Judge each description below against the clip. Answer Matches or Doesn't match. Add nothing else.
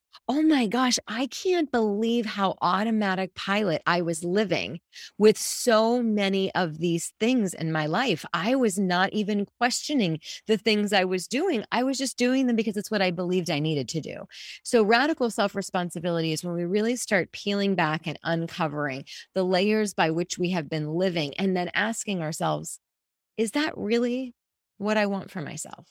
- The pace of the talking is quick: Doesn't match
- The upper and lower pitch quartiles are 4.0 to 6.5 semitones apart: Matches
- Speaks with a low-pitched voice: Doesn't match